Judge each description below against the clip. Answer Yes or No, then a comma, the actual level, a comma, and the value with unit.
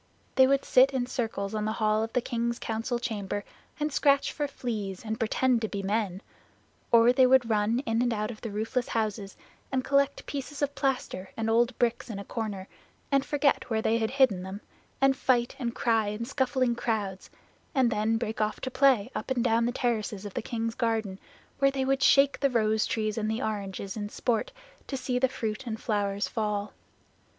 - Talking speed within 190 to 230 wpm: Yes, average, 200 wpm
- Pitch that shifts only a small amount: No, average, 3.3 semitones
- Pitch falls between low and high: No, high, 230 Hz